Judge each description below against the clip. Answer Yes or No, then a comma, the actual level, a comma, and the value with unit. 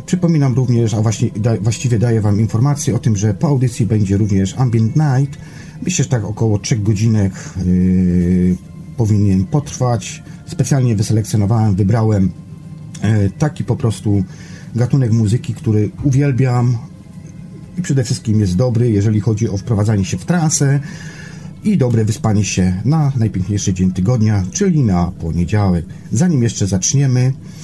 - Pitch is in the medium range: No, low, 115 Hz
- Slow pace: No, average, 130 wpm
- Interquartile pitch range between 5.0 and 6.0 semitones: Yes, wide, 5.6 semitones